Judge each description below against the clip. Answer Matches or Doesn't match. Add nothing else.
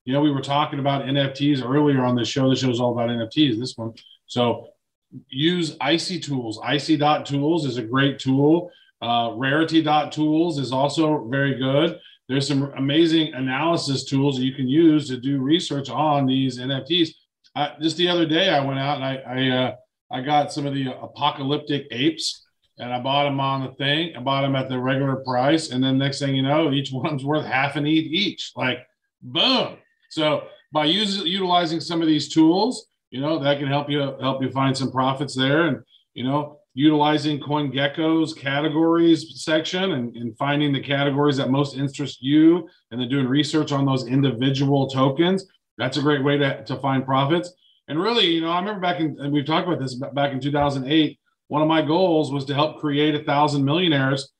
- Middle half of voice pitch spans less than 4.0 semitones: Matches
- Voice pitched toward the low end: Doesn't match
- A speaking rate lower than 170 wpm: Doesn't match